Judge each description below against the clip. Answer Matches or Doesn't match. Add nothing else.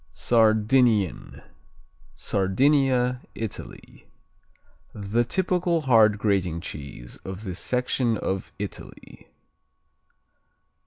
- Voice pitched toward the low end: Matches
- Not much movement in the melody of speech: Doesn't match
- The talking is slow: Matches